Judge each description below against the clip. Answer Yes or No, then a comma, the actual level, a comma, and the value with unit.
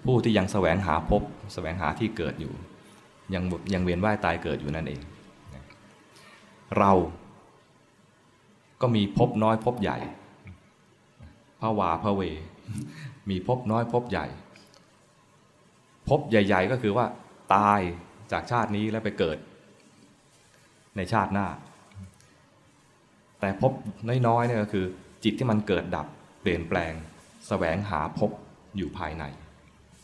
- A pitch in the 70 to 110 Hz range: Yes, low, 100 Hz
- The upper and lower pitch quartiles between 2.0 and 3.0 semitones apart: No, average, 3.7 semitones